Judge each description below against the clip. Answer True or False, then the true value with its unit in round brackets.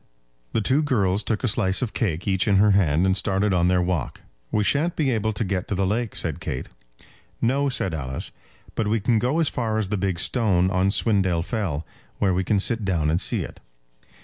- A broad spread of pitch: False (3.6 semitones)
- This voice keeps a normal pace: False (220 wpm)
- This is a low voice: True (100 Hz)